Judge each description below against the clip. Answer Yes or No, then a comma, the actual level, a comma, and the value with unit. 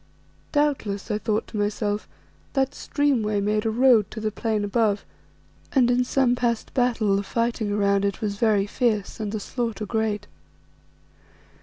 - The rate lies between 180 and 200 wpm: No, average, 155 wpm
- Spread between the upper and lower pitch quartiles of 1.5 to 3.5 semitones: Yes, average, 2.8 semitones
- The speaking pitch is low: No, high, 215 Hz